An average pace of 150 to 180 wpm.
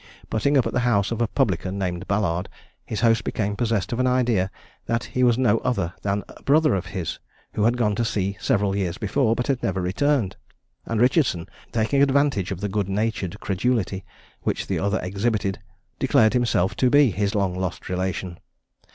No: average, 190 wpm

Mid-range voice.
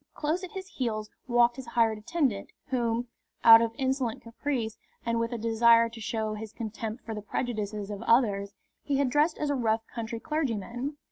No: high, 230 Hz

